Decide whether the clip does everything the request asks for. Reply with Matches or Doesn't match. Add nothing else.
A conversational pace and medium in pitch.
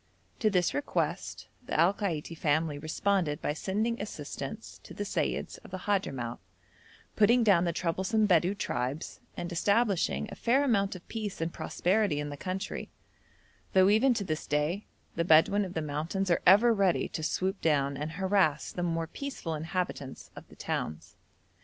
Matches